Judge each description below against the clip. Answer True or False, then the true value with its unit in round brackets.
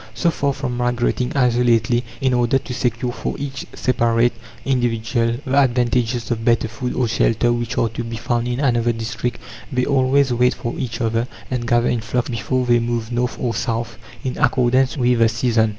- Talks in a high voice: False (120 Hz)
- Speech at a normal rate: True (185 wpm)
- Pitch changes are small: True (1.4 semitones)